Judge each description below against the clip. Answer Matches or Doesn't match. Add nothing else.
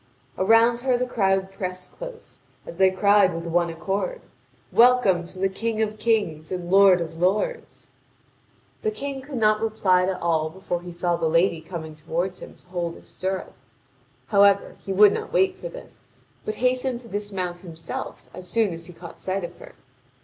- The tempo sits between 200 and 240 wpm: Doesn't match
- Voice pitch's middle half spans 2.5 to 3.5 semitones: Doesn't match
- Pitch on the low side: Doesn't match